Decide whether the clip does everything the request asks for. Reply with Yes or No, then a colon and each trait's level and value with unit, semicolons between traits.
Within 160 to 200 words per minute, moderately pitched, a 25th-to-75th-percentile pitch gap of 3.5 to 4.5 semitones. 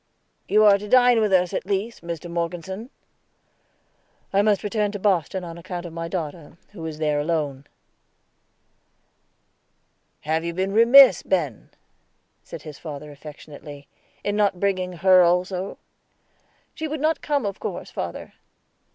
No: average, 140 wpm; medium, 180 Hz; average, 4.0 semitones